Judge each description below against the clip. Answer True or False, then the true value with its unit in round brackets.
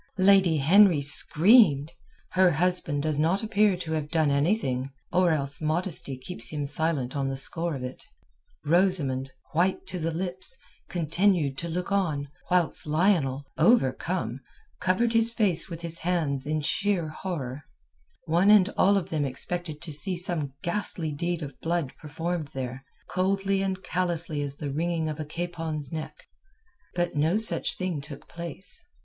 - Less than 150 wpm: False (155 wpm)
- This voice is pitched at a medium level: True (165 Hz)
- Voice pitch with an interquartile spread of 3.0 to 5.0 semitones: True (4.0 semitones)